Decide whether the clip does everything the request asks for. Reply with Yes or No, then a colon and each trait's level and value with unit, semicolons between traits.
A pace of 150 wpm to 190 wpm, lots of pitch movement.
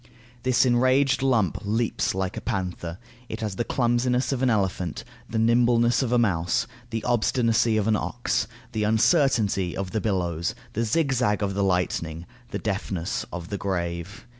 No: average, 165 wpm; average, 4.3 semitones